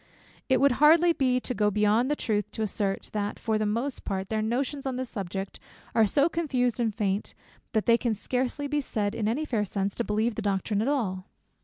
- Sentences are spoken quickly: Yes, fast, 215 wpm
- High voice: Yes, high, 225 Hz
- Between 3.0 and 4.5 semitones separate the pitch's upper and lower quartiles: Yes, average, 3.9 semitones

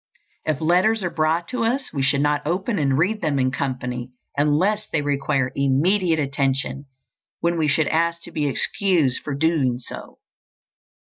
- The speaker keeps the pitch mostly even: No, average, 4.0 semitones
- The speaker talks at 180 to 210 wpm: No, average, 160 wpm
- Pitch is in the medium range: Yes, medium, 150 Hz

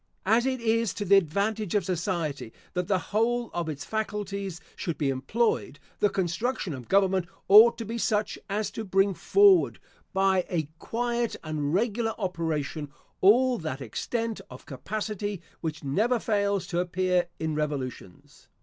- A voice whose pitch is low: No, high, 195 Hz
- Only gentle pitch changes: No, average, 5.3 semitones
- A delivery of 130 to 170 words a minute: Yes, average, 150 wpm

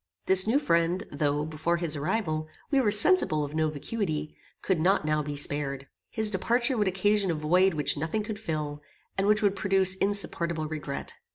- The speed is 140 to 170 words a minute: No, average, 180 wpm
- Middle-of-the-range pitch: Yes, medium, 170 Hz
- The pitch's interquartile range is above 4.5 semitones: Yes, average, 5.0 semitones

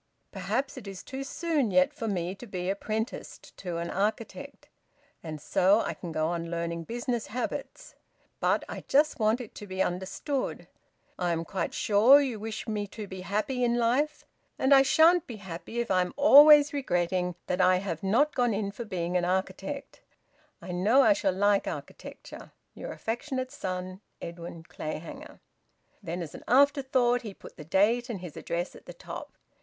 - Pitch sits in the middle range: No, high, 205 Hz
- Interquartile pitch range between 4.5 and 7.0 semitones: Yes, wide, 5.6 semitones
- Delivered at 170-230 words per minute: Yes, average, 180 wpm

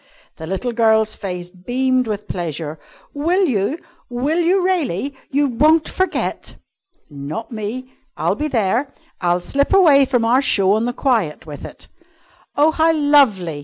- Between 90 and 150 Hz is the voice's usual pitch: No, high, 245 Hz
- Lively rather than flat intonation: Yes, wide, 7.1 semitones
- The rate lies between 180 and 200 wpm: No, average, 150 wpm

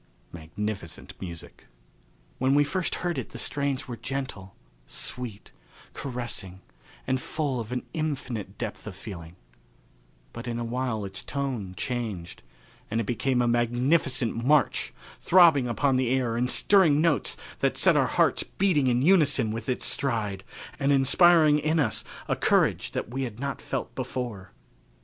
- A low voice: Yes, low, 125 Hz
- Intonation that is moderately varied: Yes, average, 4.2 semitones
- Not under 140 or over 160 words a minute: Yes, average, 155 wpm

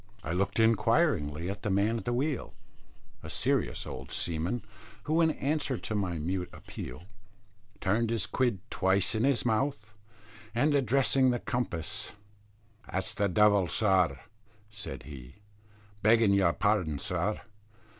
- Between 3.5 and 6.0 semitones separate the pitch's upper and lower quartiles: Yes, average, 5.2 semitones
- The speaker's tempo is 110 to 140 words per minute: Yes, slow, 135 wpm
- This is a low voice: Yes, low, 105 Hz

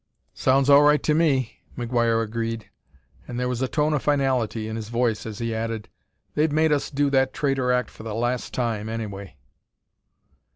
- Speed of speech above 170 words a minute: Yes, average, 180 wpm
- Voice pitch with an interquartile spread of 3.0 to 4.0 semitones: Yes, average, 3.5 semitones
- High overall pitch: No, low, 125 Hz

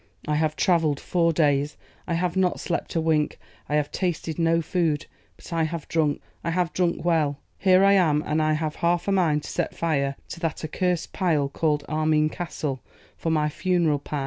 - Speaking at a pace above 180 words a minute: Yes, average, 200 wpm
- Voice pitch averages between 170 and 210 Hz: No, medium, 160 Hz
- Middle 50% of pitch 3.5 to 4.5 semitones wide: No, narrow, 2.4 semitones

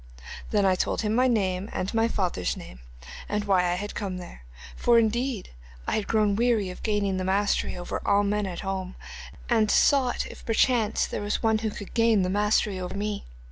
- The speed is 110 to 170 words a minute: No, average, 195 wpm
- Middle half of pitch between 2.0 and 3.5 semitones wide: Yes, average, 2.9 semitones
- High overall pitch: Yes, high, 205 Hz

